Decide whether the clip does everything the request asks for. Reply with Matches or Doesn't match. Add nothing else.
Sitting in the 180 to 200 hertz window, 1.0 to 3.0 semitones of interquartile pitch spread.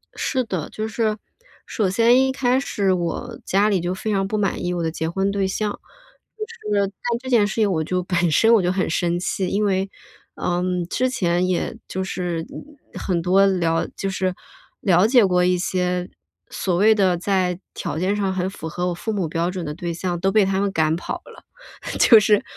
Matches